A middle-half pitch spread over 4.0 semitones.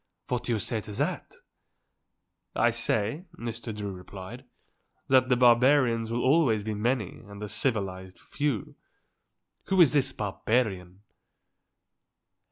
No: average, 3.7 semitones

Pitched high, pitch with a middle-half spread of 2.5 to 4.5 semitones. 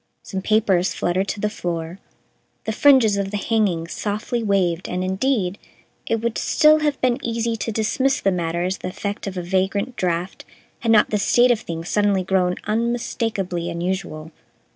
Yes: high, 200 Hz; average, 4.0 semitones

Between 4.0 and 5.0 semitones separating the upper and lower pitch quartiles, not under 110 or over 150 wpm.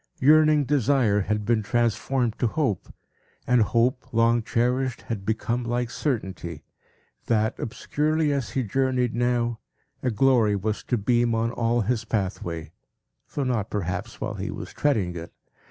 No: average, 3.2 semitones; average, 145 wpm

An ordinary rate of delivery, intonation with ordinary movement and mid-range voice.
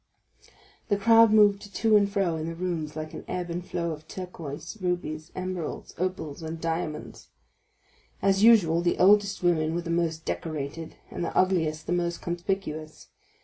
Yes: average, 160 wpm; average, 3.2 semitones; medium, 175 Hz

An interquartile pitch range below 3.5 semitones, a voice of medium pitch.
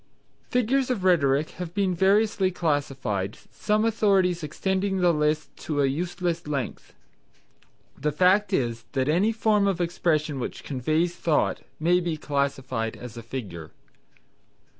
No: wide, 5.4 semitones; medium, 165 Hz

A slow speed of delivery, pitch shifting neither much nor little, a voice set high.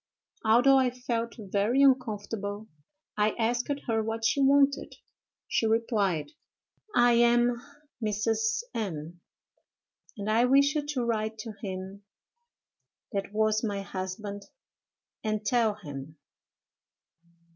Yes: slow, 110 wpm; average, 3.1 semitones; high, 220 Hz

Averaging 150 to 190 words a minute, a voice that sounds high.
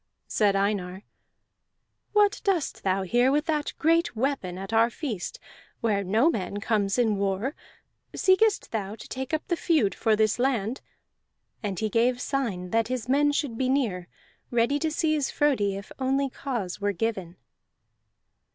Yes: average, 155 wpm; high, 230 Hz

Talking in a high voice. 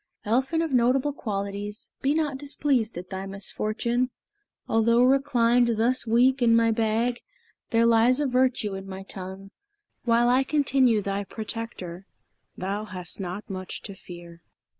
Yes: high, 230 Hz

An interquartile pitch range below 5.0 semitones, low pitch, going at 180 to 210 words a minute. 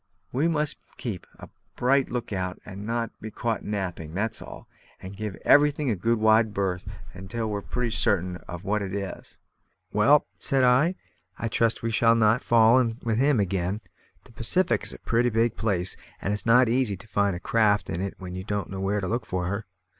Yes: average, 3.3 semitones; low, 110 Hz; fast, 205 wpm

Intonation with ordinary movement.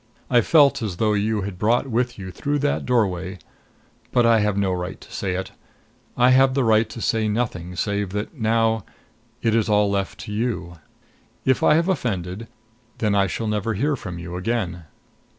Yes: average, 3.8 semitones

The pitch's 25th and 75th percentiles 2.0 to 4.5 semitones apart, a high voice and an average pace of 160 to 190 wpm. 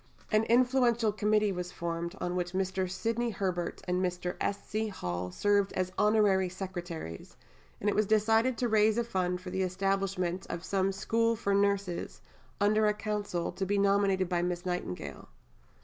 Yes: average, 2.9 semitones; high, 195 Hz; average, 165 wpm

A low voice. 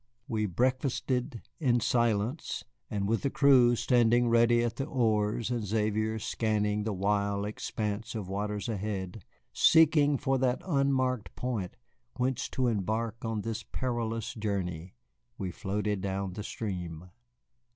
Yes: low, 110 Hz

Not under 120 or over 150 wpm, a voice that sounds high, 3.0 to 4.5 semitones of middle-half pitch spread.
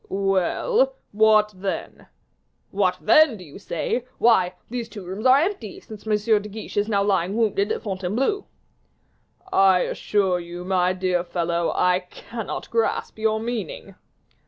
Yes: average, 145 wpm; high, 205 Hz; average, 3.3 semitones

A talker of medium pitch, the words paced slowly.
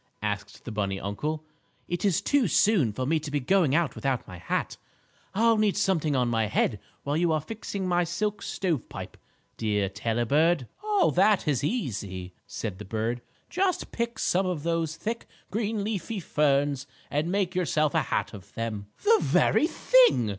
No: medium, 155 Hz; average, 175 wpm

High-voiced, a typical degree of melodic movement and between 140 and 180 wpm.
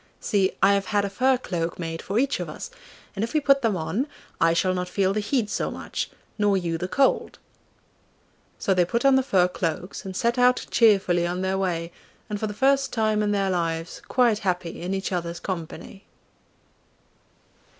No: high, 195 Hz; average, 4.1 semitones; average, 195 wpm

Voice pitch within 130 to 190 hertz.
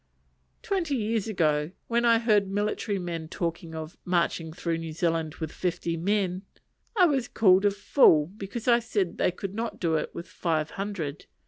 Yes: medium, 185 Hz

